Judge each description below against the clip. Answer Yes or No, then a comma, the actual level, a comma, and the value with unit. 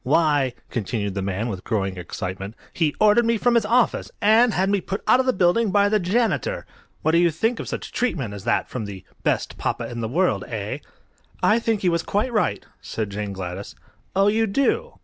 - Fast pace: Yes, fast, 210 wpm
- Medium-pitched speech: Yes, medium, 175 Hz